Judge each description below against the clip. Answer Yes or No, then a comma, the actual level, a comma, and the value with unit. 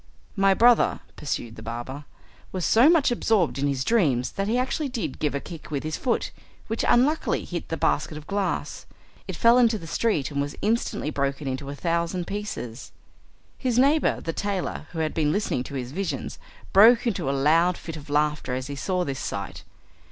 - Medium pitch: Yes, medium, 165 Hz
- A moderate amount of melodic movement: No, wide, 7.8 semitones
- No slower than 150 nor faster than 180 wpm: No, average, 195 wpm